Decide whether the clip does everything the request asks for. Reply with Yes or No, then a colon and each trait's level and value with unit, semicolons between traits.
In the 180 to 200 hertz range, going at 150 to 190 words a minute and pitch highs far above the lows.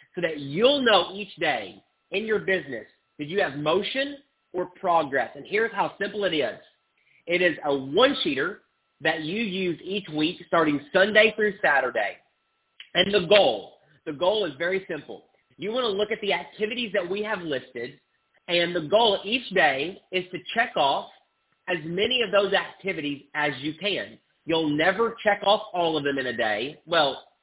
No: medium, 185 Hz; average, 175 wpm; average, 4.7 semitones